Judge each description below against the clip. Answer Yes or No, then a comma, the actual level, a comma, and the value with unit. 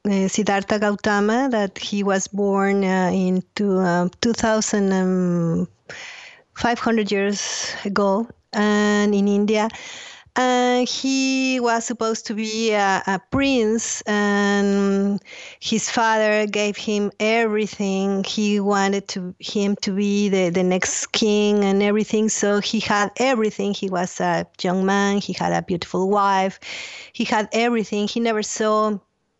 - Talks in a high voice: Yes, high, 205 Hz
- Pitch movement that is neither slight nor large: No, narrow, 1.9 semitones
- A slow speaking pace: Yes, slow, 130 wpm